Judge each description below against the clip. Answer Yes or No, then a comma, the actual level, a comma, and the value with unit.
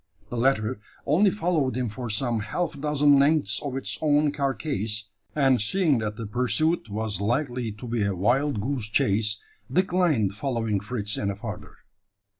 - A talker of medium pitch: No, low, 125 Hz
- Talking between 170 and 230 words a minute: No, average, 155 wpm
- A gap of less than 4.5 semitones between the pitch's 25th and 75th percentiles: No, wide, 5.4 semitones